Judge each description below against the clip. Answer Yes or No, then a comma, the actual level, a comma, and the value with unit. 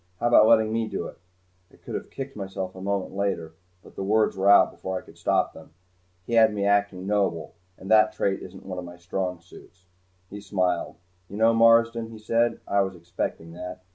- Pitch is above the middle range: No, low, 100 Hz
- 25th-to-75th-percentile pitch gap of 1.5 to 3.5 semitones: Yes, average, 3.1 semitones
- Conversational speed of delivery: No, fast, 210 wpm